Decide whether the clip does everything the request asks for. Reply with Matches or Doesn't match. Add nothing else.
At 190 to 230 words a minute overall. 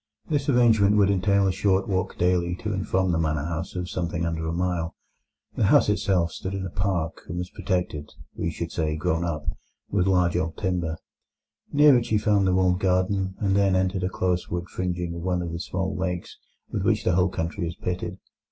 Matches